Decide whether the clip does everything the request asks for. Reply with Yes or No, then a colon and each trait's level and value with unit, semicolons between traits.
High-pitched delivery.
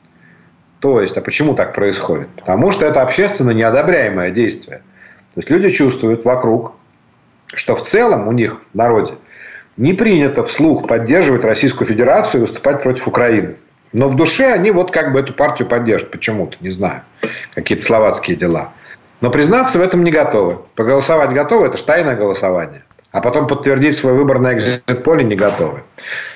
No: low, 135 Hz